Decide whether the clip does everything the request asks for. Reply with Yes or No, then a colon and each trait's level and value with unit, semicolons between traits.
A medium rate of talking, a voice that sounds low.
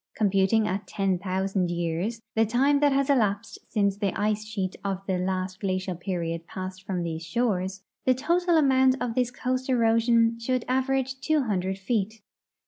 No: average, 165 wpm; high, 210 Hz